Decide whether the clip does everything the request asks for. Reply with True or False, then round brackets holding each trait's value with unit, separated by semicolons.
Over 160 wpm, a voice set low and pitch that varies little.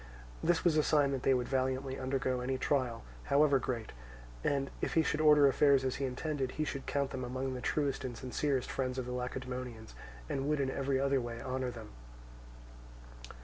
True (190 wpm; 130 Hz; 1.7 semitones)